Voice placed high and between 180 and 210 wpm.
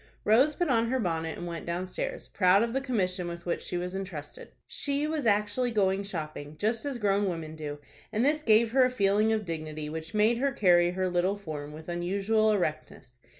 Yes: high, 195 Hz; average, 200 wpm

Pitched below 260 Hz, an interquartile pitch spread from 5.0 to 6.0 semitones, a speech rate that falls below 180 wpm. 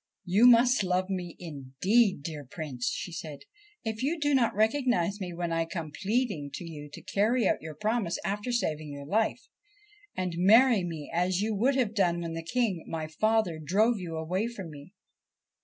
No: medium, 185 Hz; average, 5.3 semitones; average, 190 wpm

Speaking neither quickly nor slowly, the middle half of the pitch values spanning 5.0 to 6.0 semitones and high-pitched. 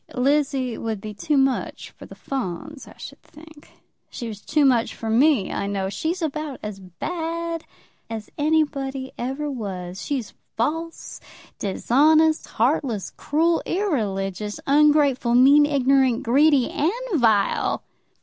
No: slow, 130 wpm; wide, 5.4 semitones; very high, 270 Hz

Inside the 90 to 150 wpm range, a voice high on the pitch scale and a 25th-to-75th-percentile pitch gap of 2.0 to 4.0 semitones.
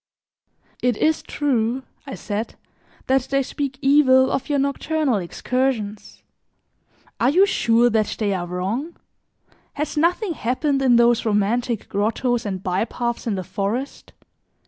No: slow, 135 wpm; high, 245 Hz; average, 4.5 semitones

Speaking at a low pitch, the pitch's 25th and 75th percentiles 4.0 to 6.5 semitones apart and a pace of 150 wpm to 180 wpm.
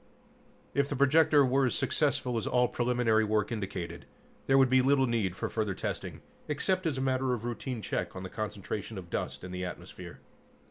No: low, 120 Hz; average, 4.9 semitones; average, 190 wpm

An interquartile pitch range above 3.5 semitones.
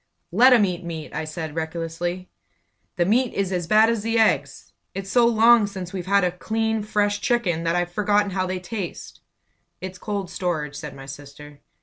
Yes: average, 4.0 semitones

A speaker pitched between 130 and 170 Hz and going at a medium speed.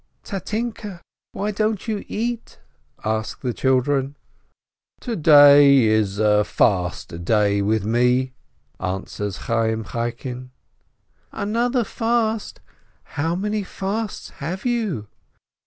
No: medium, 140 Hz; slow, 100 wpm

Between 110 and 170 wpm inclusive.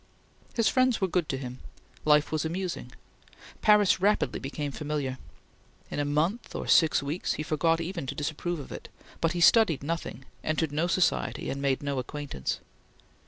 Yes: average, 165 wpm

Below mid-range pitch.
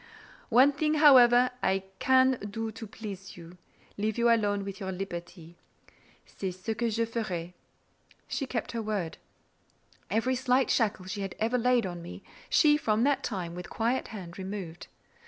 No: high, 215 Hz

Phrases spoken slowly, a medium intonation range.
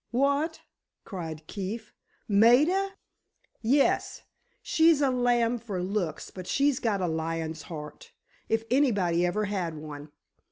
No: slow, 115 wpm; wide, 7.6 semitones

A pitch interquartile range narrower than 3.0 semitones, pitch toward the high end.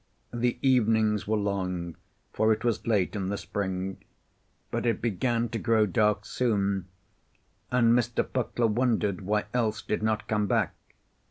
No: narrow, 2.6 semitones; low, 110 Hz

